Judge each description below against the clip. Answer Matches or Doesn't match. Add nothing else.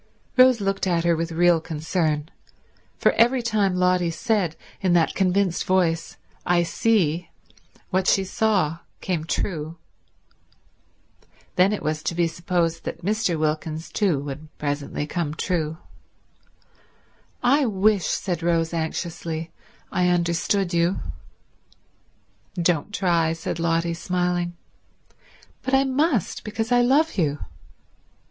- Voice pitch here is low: Doesn't match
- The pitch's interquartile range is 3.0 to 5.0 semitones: Matches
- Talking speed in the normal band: Doesn't match